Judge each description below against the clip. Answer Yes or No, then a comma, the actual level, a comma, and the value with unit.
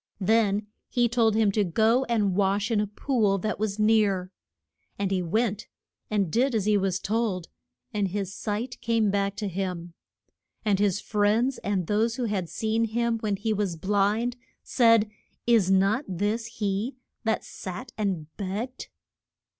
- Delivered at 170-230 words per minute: No, average, 160 wpm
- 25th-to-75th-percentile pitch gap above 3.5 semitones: No, narrow, 2.6 semitones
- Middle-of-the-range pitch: No, high, 210 Hz